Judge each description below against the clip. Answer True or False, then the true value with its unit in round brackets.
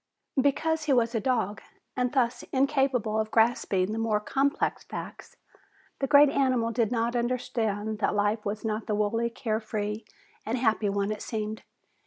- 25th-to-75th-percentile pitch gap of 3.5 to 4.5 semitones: False (3.0 semitones)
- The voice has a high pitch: True (225 Hz)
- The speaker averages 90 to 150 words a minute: False (160 wpm)